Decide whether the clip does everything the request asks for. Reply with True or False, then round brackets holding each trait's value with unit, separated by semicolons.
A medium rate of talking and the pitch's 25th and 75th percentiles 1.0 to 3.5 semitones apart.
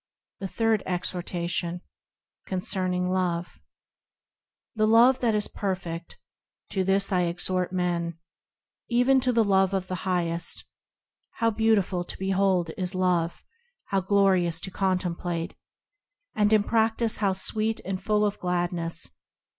False (125 wpm; 2.9 semitones)